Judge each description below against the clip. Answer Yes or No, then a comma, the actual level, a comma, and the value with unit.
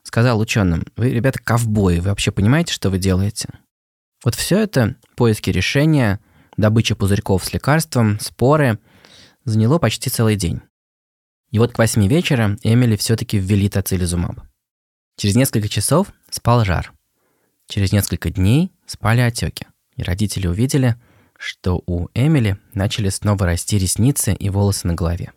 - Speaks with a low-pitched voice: Yes, low, 105 Hz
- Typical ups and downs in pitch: Yes, average, 4.0 semitones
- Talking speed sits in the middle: Yes, average, 135 wpm